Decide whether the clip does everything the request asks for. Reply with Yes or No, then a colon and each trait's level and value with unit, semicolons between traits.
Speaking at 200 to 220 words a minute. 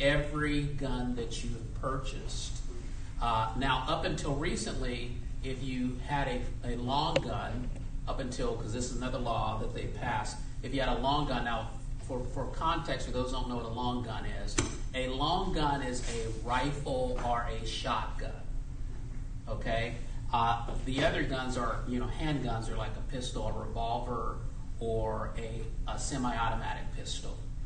No: average, 165 wpm